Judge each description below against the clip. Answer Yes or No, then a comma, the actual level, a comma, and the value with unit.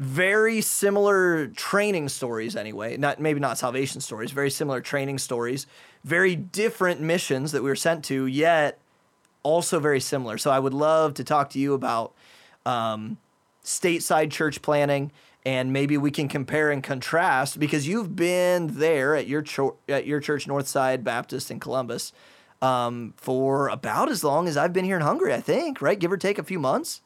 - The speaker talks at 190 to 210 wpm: No, average, 175 wpm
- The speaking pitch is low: No, medium, 145 Hz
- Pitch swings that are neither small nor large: Yes, average, 4.1 semitones